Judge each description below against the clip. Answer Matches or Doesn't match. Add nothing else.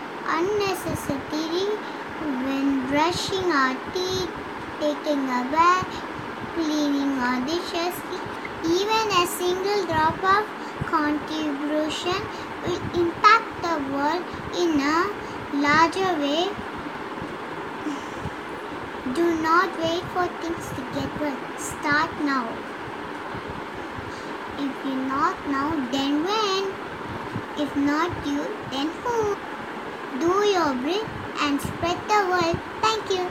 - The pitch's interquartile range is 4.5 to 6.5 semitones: Doesn't match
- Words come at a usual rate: Matches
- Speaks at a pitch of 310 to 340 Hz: Matches